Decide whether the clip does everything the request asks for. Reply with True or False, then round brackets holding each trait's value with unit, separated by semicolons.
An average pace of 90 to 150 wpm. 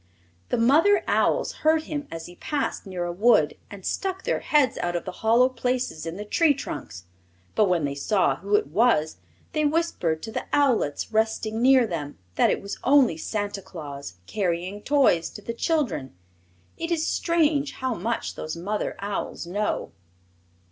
False (170 wpm)